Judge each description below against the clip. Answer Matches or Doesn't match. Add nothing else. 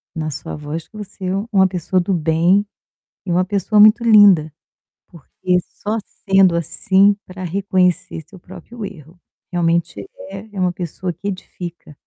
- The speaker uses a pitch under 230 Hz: Matches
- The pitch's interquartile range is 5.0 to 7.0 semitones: Doesn't match